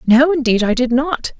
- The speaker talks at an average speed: No, fast, 215 wpm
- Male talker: No, female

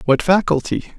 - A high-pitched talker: No, medium, 160 Hz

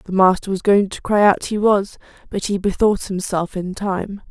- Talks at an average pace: No, fast, 210 wpm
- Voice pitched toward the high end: Yes, high, 195 Hz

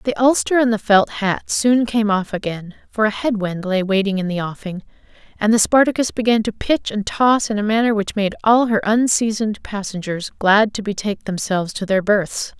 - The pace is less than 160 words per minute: No, fast, 205 wpm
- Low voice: No, high, 210 Hz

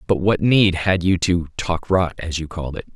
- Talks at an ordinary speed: No, fast, 245 wpm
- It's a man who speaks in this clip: Yes, male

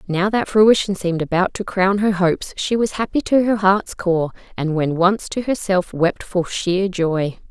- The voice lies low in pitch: No, high, 190 Hz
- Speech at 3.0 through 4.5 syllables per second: Yes, 4.4 syllables/s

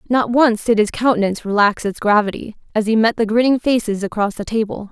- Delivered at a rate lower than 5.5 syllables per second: No, 6.0 syllables/s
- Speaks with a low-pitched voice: No, high, 220 Hz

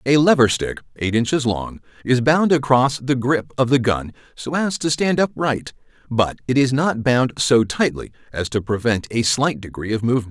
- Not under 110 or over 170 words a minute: No, average, 200 wpm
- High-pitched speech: No, low, 125 Hz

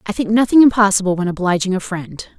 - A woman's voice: Yes, female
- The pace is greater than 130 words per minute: Yes, average, 200 wpm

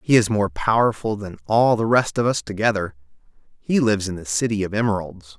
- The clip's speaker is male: Yes, male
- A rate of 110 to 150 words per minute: No, average, 200 wpm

